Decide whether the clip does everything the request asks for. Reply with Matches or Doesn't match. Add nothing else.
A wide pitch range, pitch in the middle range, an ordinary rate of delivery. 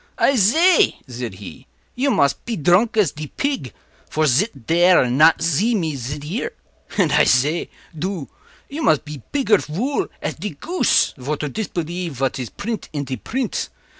Matches